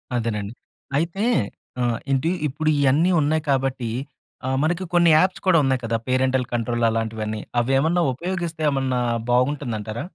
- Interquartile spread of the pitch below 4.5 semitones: No, average, 5.0 semitones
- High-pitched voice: No, low, 130 Hz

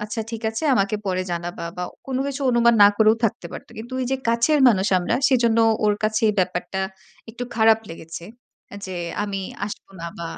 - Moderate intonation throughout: Yes, average, 4.2 semitones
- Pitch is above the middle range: Yes, high, 215 Hz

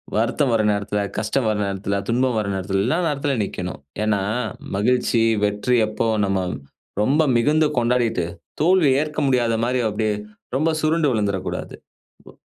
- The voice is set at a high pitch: No, low, 115 Hz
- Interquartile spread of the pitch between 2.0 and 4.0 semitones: No, average, 4.8 semitones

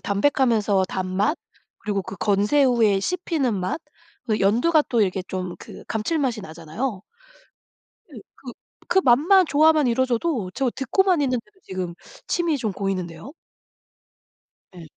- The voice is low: No, high, 230 Hz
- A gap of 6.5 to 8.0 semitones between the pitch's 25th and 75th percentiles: Yes, wide, 6.8 semitones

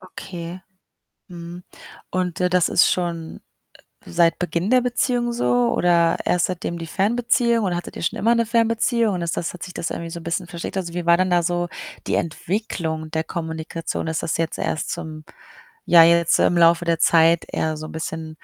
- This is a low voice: No, medium, 170 Hz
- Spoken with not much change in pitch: Yes, narrow, 2.0 semitones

